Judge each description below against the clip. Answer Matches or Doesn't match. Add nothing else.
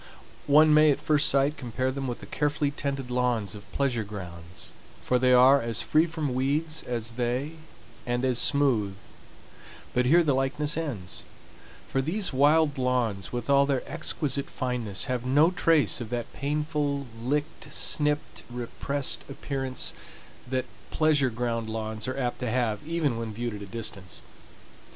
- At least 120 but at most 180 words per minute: Matches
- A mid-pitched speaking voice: Doesn't match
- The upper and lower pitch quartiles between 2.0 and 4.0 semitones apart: Matches